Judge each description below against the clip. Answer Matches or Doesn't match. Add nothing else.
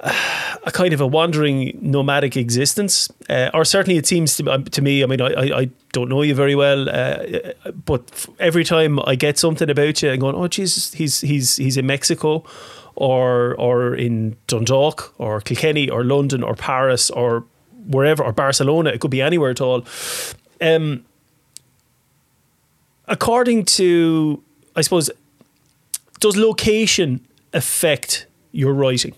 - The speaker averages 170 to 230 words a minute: Doesn't match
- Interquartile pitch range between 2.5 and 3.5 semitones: Doesn't match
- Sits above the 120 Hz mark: Matches